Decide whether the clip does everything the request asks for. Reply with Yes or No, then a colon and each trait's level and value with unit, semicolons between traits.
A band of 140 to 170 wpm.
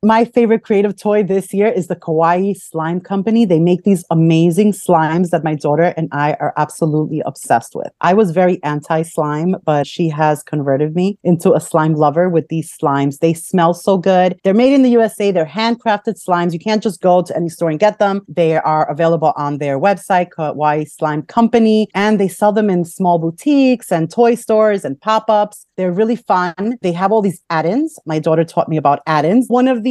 No: fast, 205 wpm